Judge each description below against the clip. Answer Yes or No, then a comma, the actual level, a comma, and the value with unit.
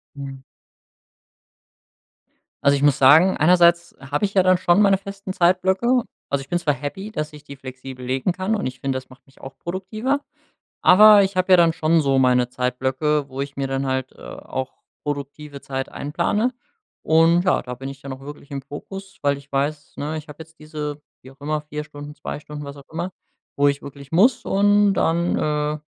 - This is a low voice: No, medium, 150 Hz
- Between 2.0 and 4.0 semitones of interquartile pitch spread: No, average, 4.8 semitones